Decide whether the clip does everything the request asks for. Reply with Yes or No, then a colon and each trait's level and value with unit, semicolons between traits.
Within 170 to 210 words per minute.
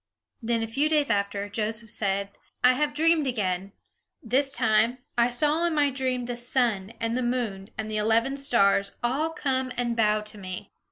Yes: average, 175 wpm